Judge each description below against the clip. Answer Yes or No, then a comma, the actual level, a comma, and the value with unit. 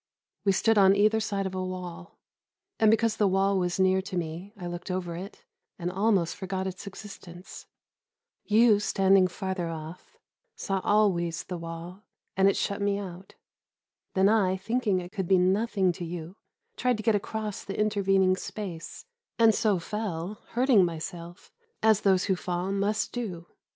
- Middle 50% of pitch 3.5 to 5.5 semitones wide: No, average, 2.7 semitones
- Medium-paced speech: Yes, average, 165 wpm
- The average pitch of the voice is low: No, high, 190 Hz